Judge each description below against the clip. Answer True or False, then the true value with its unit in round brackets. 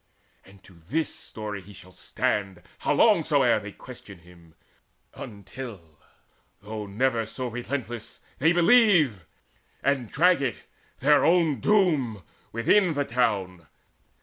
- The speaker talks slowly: True (120 wpm)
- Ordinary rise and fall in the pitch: False (6.7 semitones)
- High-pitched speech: False (115 Hz)